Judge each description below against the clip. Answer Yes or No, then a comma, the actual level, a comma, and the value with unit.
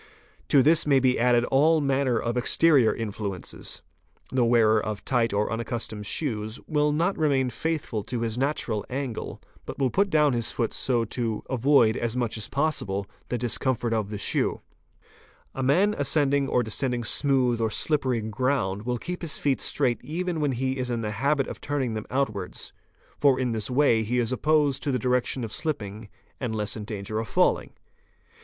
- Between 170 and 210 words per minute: Yes, average, 185 wpm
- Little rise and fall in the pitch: No, average, 4.1 semitones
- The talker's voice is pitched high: No, low, 125 Hz